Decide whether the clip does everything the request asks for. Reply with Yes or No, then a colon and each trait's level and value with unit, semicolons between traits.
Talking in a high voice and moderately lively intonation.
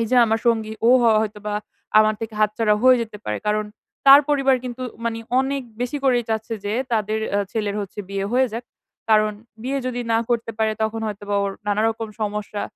No: high, 220 Hz; narrow, 2.3 semitones